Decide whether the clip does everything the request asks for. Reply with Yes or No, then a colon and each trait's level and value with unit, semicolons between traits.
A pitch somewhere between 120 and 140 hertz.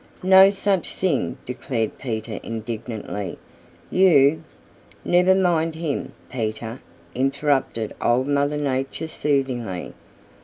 Yes: low, 135 Hz